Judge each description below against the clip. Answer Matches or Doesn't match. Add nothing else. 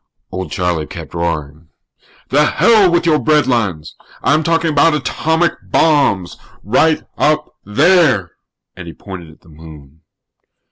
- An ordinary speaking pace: Doesn't match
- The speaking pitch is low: Matches